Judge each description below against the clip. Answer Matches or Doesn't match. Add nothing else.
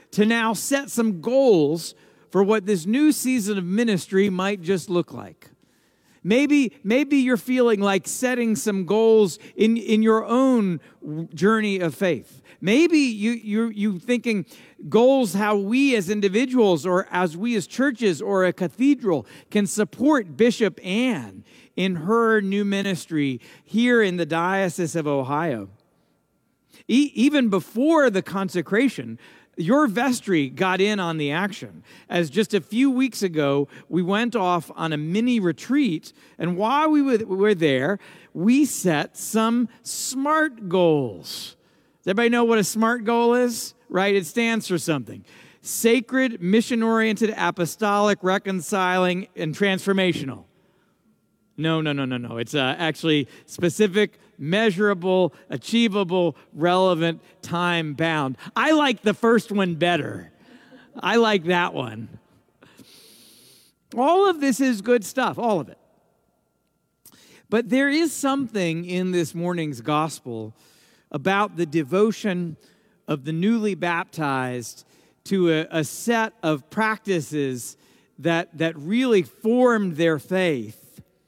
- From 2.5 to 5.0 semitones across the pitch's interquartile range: Doesn't match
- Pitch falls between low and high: Doesn't match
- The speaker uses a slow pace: Matches